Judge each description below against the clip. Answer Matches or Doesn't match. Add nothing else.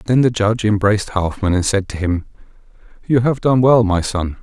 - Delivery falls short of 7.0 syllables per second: Matches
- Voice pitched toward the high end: Doesn't match